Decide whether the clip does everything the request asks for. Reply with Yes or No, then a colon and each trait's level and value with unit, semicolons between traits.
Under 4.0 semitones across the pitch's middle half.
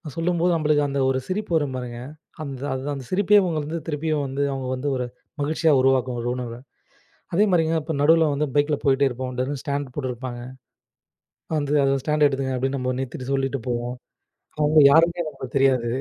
Yes: average, 3.2 semitones